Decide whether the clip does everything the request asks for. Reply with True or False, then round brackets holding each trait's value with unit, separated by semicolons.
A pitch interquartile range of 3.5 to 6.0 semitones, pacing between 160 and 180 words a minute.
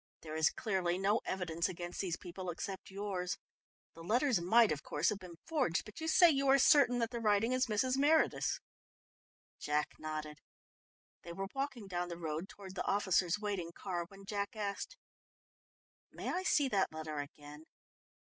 True (5.3 semitones; 170 wpm)